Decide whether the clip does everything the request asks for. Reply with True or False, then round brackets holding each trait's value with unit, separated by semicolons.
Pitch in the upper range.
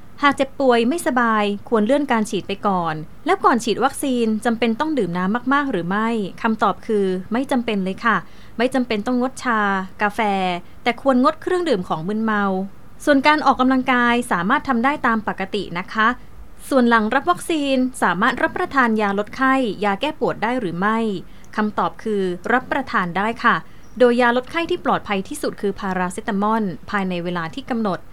True (230 Hz)